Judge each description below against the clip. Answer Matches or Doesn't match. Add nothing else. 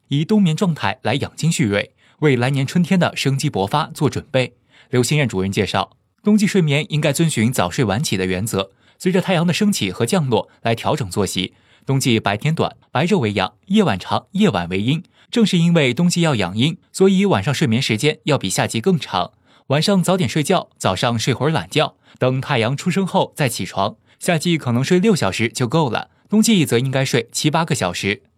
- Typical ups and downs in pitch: Doesn't match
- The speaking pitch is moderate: Matches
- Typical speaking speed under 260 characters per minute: Doesn't match